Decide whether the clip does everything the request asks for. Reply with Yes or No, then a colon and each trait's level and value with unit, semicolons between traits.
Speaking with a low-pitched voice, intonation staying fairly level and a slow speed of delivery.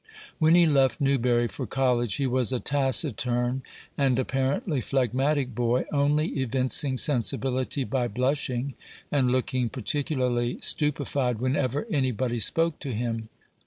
Yes: low, 130 Hz; narrow, 2.3 semitones; slow, 125 wpm